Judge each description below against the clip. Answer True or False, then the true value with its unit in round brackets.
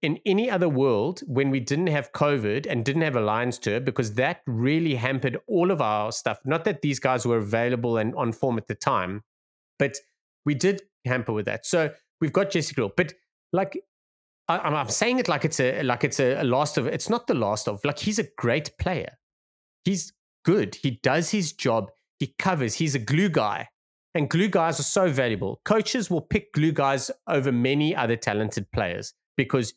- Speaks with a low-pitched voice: False (145 Hz)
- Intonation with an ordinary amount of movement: False (6.5 semitones)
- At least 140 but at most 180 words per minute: False (200 wpm)